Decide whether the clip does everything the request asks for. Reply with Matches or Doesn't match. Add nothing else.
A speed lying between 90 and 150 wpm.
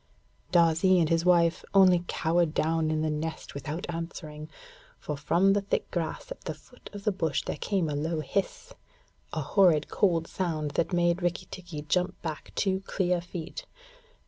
Doesn't match